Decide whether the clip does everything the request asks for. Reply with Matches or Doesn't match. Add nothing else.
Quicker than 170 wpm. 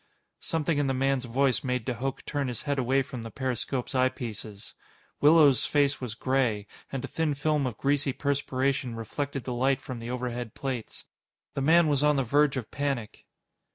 Matches